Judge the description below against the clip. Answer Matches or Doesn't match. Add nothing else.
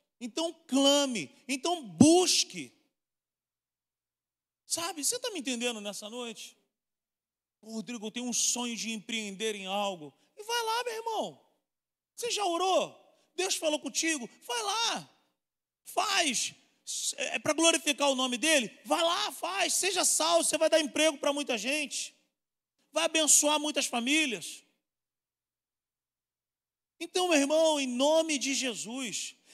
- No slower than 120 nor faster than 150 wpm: Matches